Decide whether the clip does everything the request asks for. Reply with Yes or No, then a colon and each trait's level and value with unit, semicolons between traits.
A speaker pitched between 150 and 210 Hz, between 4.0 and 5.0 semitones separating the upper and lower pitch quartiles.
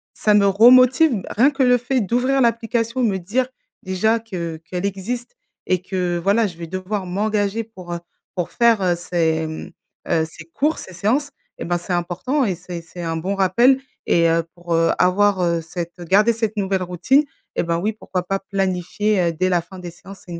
Yes: high, 190 Hz; average, 4.6 semitones